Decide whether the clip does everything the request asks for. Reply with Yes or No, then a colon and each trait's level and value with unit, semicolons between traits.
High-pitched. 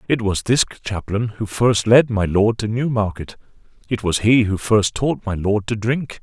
No: low, 110 Hz